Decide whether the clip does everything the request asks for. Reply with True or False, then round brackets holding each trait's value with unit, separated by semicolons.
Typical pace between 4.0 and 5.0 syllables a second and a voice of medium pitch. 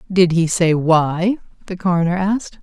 True (4.7 syllables/s; 180 Hz)